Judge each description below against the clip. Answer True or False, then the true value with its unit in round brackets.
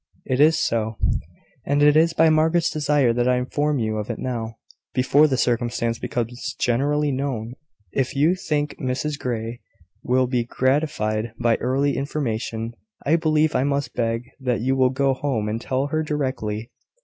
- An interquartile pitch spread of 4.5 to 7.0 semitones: False (3.9 semitones)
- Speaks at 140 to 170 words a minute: True (165 wpm)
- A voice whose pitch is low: True (130 Hz)